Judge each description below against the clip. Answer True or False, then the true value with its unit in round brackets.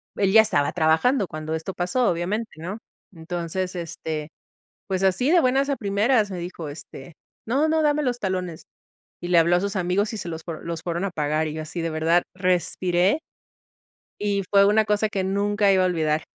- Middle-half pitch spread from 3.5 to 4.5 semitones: True (3.8 semitones)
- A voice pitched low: False (185 Hz)